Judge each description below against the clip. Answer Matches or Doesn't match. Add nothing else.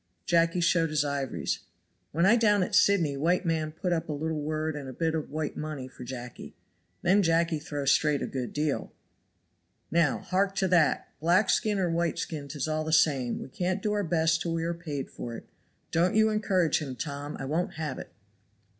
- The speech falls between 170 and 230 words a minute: Matches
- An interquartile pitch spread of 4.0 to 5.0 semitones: Doesn't match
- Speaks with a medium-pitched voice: Matches